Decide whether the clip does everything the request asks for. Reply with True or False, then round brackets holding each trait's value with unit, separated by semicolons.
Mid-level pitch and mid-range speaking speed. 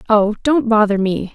False (215 Hz; 180 wpm)